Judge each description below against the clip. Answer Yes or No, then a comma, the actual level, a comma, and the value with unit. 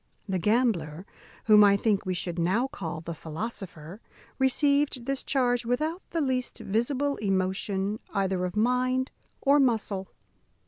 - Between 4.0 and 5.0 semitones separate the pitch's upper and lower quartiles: No, wide, 5.4 semitones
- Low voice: No, high, 215 Hz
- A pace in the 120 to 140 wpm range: Yes, slow, 135 wpm